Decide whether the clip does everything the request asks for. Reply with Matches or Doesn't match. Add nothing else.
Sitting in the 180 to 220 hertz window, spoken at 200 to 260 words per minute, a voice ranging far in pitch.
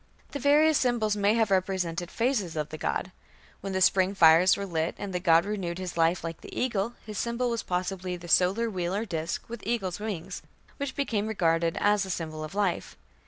Doesn't match